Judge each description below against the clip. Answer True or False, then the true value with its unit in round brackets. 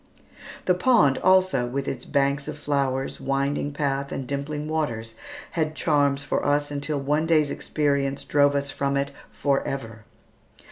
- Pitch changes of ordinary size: False (1.4 semitones)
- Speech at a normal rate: True (145 wpm)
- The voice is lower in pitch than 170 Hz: True (140 Hz)